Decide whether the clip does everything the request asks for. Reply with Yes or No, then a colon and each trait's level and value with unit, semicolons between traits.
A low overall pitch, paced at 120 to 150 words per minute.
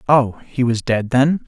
No: low, 125 Hz; fast, 205 wpm